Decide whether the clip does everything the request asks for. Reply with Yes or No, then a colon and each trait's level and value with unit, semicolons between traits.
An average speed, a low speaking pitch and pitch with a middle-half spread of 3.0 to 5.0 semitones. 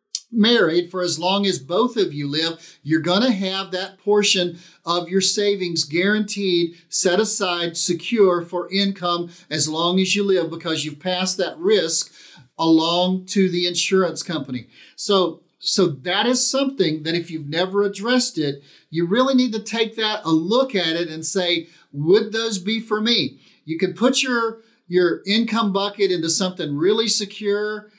No: average, 165 wpm; medium, 185 Hz; average, 3.7 semitones